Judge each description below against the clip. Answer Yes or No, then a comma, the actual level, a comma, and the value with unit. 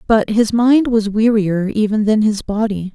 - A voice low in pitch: No, high, 215 Hz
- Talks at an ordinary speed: Yes, average, 185 wpm